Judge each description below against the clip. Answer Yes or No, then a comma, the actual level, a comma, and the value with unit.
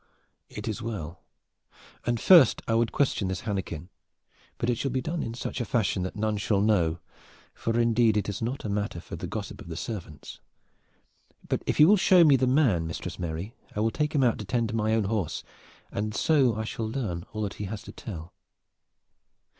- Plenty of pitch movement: No, average, 3.6 semitones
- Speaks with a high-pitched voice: No, low, 110 Hz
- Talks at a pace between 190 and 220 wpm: Yes, average, 200 wpm